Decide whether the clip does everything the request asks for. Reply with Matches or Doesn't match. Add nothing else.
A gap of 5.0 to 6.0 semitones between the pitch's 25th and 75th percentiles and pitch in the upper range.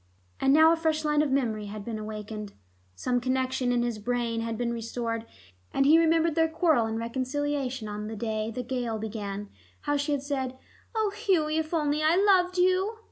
Matches